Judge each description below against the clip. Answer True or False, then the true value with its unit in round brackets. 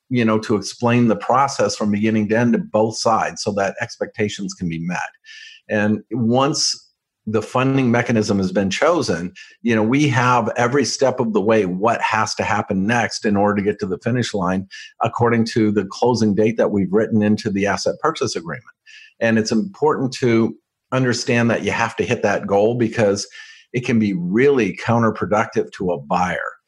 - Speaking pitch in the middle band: False (110 Hz)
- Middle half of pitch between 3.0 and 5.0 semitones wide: False (2.6 semitones)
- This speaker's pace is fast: False (185 wpm)